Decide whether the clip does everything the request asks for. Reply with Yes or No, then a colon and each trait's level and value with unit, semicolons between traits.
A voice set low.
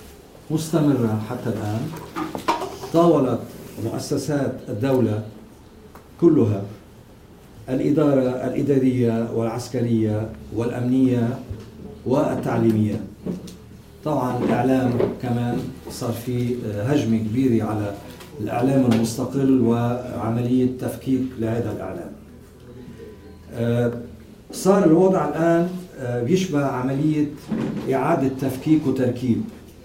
Yes: low, 125 Hz